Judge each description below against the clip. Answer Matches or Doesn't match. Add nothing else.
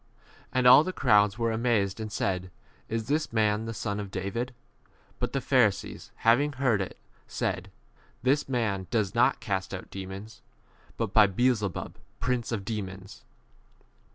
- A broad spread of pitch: Doesn't match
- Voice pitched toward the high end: Doesn't match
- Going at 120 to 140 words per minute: Doesn't match